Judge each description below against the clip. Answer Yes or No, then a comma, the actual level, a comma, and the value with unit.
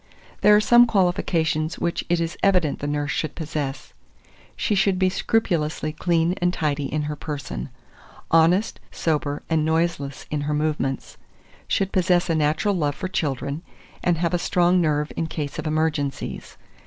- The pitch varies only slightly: No, average, 3.1 semitones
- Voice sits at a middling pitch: Yes, medium, 160 Hz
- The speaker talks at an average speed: Yes, average, 160 wpm